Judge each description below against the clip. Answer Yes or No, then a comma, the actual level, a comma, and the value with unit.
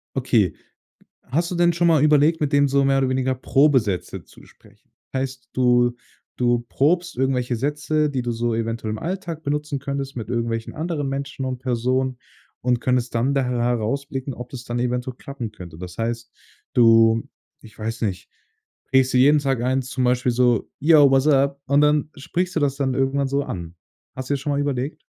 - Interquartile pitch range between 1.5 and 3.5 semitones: Yes, average, 2.9 semitones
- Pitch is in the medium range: No, low, 130 Hz